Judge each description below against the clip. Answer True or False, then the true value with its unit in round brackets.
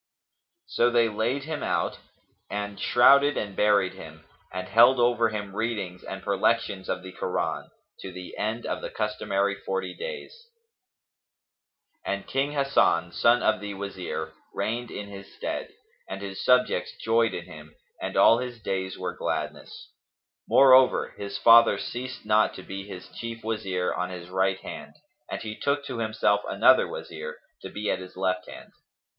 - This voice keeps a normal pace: True (160 wpm)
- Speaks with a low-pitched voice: True (105 Hz)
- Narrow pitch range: False (4.0 semitones)